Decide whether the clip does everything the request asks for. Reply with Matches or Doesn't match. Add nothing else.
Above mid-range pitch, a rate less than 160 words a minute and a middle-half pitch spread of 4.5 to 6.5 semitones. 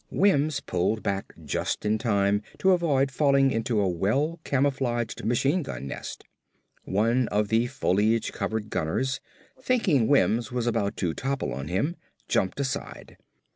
Doesn't match